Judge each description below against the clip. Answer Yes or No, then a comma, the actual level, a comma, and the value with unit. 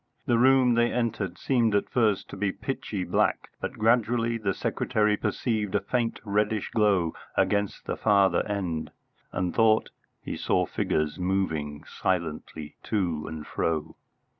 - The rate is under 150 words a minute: Yes, average, 140 wpm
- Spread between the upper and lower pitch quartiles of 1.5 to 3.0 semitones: No, average, 4.4 semitones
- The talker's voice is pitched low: Yes, low, 100 Hz